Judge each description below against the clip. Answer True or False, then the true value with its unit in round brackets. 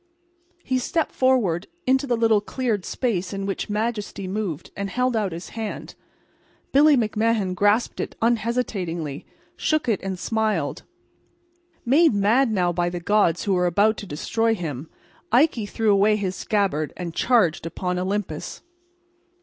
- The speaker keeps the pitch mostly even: False (4.3 semitones)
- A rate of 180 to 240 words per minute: False (145 wpm)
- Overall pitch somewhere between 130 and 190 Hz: False (205 Hz)